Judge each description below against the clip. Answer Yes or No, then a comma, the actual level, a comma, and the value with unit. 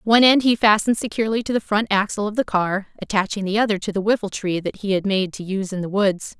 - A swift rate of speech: Yes, fast, 255 wpm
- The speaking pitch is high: Yes, high, 205 Hz